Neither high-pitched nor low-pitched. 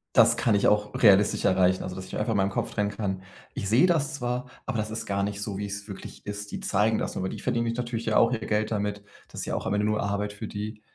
No: low, 105 Hz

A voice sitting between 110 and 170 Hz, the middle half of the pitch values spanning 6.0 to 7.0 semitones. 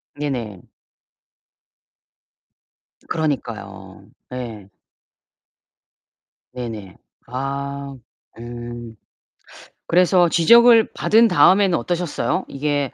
Yes: medium, 140 Hz; wide, 6.7 semitones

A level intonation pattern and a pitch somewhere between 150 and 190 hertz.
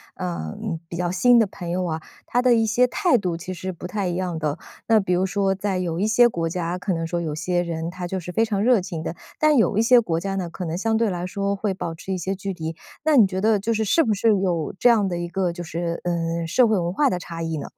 No: average, 3.9 semitones; medium, 185 Hz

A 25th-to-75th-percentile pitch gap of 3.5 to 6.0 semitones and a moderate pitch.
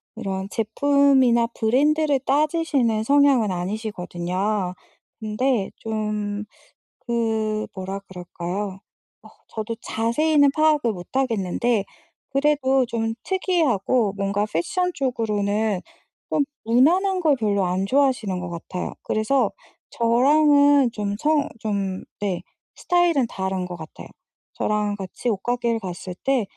No: wide, 5.5 semitones; high, 225 Hz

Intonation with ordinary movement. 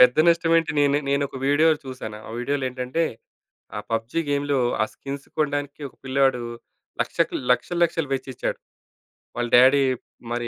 No: narrow, 2.3 semitones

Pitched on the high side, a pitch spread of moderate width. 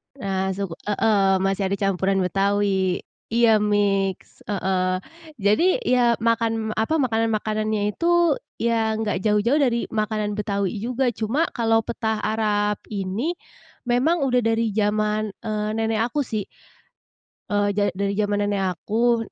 No: high, 215 Hz; narrow, 2.3 semitones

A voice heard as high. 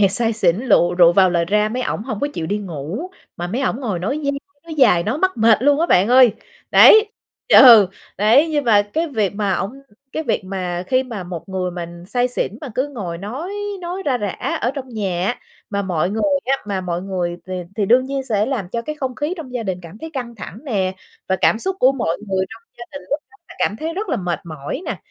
Yes: high, 220 Hz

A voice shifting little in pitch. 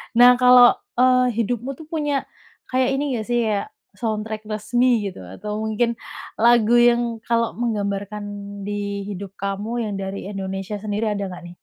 No: average, 3.0 semitones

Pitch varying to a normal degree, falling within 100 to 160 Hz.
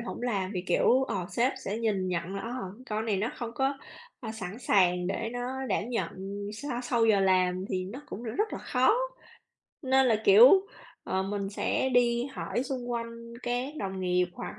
No: average, 4.4 semitones; high, 225 Hz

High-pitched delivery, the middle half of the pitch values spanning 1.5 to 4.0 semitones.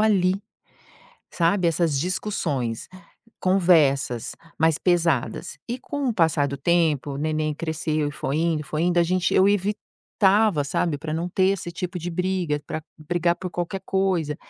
No: medium, 170 Hz; average, 3.4 semitones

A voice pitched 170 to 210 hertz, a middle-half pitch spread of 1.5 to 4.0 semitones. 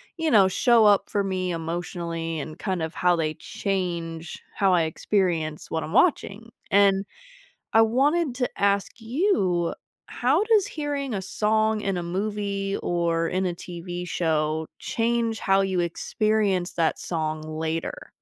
No: high, 190 Hz; average, 4.4 semitones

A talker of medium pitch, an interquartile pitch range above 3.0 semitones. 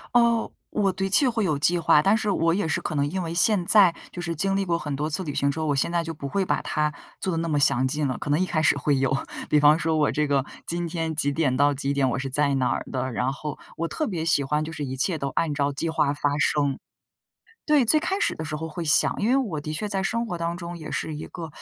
Yes: medium, 160 Hz; average, 3.6 semitones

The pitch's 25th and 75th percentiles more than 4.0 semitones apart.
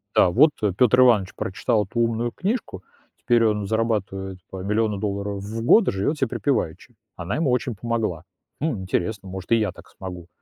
No: average, 3.5 semitones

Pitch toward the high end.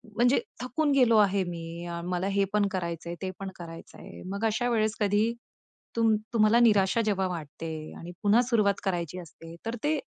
Yes: high, 200 Hz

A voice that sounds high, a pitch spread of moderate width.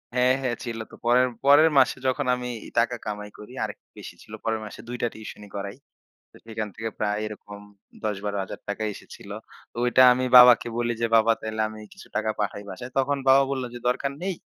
No: low, 115 Hz; average, 3.1 semitones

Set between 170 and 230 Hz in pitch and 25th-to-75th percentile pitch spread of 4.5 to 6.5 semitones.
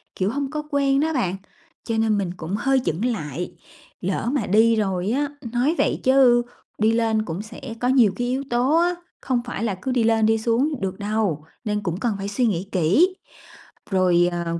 Yes: high, 225 Hz; average, 4.9 semitones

